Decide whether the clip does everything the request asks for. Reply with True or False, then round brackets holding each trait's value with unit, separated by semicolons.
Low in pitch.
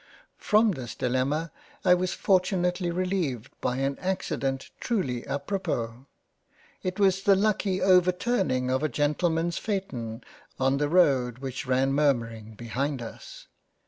False (145 Hz)